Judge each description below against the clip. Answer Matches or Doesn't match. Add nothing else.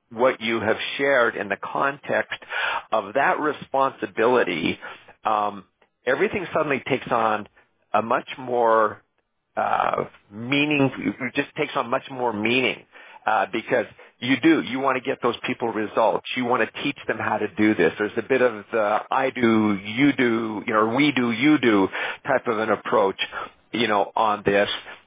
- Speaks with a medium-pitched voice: Doesn't match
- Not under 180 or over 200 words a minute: Doesn't match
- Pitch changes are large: Doesn't match